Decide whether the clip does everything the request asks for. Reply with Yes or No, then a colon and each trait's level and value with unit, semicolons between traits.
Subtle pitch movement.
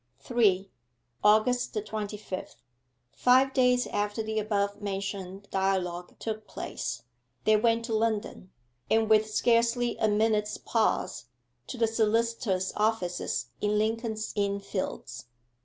Yes: narrow, 2.2 semitones